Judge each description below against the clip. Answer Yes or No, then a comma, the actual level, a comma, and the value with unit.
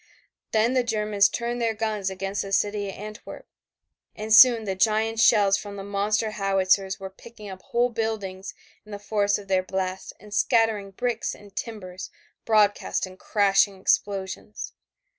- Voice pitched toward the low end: No, high, 205 Hz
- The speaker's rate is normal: Yes, average, 160 wpm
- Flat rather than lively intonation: Yes, narrow, 2.1 semitones